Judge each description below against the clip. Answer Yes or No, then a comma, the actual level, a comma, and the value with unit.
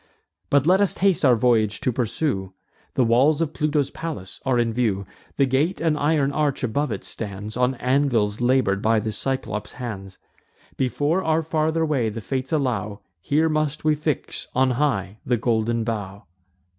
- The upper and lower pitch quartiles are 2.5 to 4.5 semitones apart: No, average, 5.3 semitones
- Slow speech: No, average, 170 wpm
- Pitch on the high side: No, low, 130 Hz